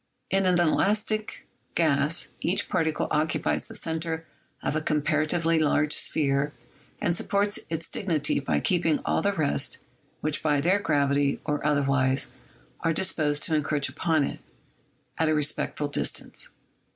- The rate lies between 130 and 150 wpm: Yes, average, 140 wpm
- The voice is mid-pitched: Yes, medium, 155 Hz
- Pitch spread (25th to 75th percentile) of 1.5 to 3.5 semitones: Yes, narrow, 2.6 semitones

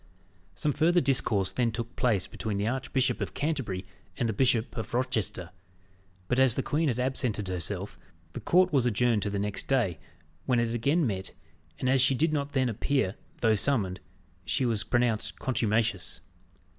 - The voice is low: Yes, low, 120 Hz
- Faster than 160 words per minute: Yes, average, 170 wpm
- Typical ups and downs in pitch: Yes, average, 4.2 semitones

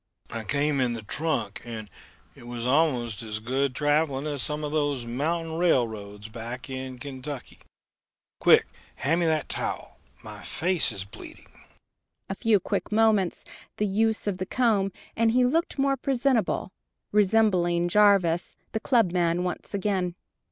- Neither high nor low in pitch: Yes, medium, 160 Hz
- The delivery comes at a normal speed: Yes, average, 145 wpm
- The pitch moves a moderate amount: No, wide, 7.7 semitones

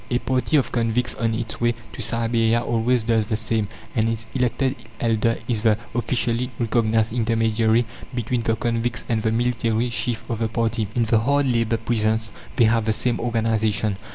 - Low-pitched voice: Yes, low, 115 Hz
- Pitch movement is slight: Yes, narrow, 1.3 semitones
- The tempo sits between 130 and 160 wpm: No, average, 180 wpm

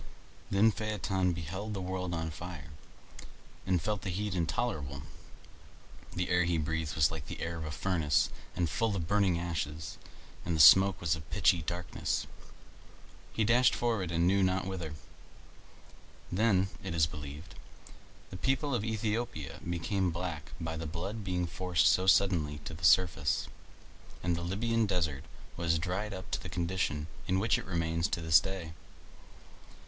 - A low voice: Yes, very low, 90 Hz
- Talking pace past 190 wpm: No, average, 160 wpm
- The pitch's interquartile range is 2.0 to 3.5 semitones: Yes, average, 3.1 semitones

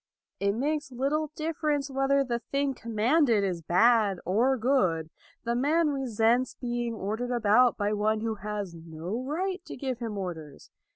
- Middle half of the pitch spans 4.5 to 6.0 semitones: Yes, average, 4.8 semitones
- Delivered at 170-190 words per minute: No, average, 155 wpm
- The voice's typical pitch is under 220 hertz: No, high, 235 Hz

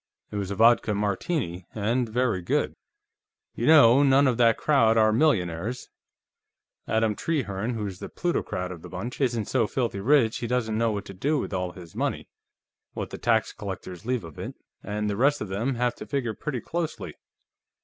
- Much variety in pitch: No, average, 4.1 semitones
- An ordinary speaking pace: Yes, average, 185 wpm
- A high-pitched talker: No, low, 115 Hz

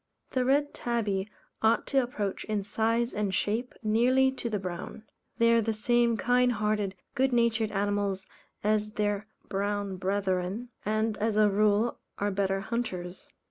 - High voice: Yes, high, 215 Hz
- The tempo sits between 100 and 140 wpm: No, average, 150 wpm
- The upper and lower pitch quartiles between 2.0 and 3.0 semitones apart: Yes, narrow, 2.6 semitones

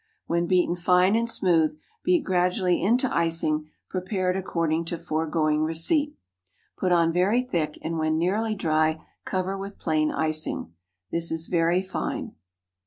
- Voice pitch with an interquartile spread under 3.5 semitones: Yes, average, 2.9 semitones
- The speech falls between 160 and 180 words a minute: No, average, 140 wpm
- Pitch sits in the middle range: Yes, medium, 170 Hz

